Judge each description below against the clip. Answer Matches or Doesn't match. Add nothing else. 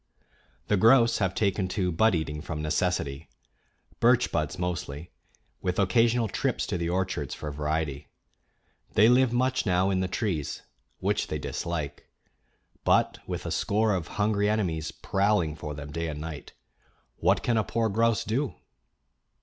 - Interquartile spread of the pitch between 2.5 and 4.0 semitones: Doesn't match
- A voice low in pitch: Matches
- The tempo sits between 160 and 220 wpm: Doesn't match